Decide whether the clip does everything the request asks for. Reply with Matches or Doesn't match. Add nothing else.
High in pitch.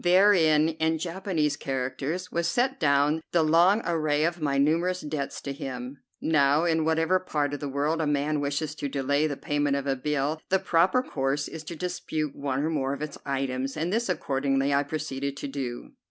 Doesn't match